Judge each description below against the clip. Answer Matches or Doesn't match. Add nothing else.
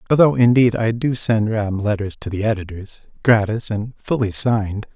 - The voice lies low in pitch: Matches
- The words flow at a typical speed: Matches